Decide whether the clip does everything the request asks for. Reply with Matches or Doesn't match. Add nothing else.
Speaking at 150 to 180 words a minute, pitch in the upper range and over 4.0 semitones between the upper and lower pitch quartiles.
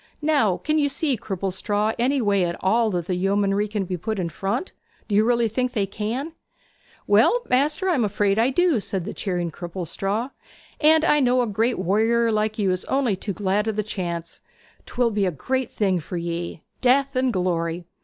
Doesn't match